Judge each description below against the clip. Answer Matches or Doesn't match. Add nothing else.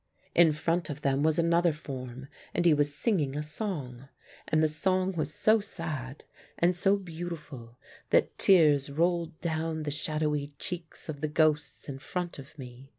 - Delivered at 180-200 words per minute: Doesn't match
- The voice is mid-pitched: Matches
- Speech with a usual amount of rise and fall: Matches